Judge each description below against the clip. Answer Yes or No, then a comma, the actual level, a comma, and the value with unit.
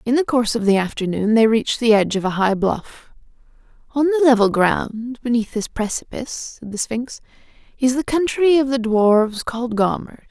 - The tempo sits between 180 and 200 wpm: Yes, average, 185 wpm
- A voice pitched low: No, high, 235 Hz